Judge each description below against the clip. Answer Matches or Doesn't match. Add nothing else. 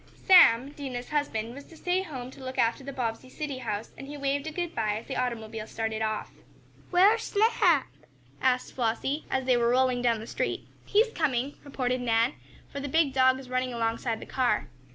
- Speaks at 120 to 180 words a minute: Doesn't match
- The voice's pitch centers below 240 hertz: Doesn't match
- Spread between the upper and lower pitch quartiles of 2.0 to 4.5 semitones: Matches